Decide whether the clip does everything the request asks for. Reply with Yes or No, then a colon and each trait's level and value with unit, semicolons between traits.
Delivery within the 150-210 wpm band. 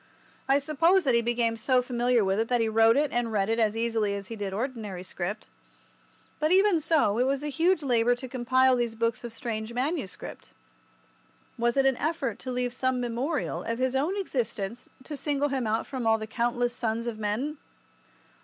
Yes: average, 200 wpm